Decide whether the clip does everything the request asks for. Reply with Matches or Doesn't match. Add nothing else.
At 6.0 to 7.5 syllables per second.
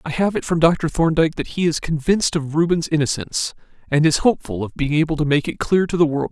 Matches